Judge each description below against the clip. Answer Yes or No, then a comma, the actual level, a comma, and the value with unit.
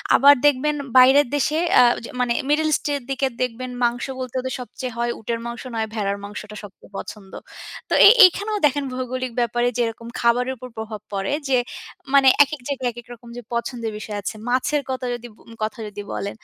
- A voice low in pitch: No, high, 245 Hz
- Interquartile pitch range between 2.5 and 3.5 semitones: Yes, average, 2.9 semitones